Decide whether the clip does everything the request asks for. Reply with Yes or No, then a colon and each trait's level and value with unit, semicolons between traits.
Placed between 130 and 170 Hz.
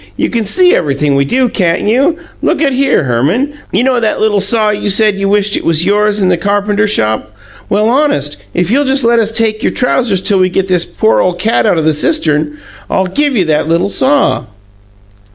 No: high, 205 Hz